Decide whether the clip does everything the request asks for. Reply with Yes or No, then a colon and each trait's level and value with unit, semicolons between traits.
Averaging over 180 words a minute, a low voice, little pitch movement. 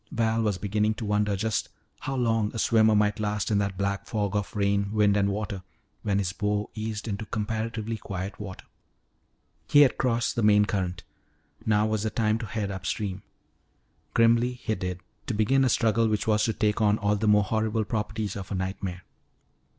Yes: average, 190 wpm; low, 105 Hz; narrow, 1.7 semitones